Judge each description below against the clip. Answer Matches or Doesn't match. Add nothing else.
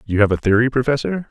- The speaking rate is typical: Doesn't match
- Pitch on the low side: Matches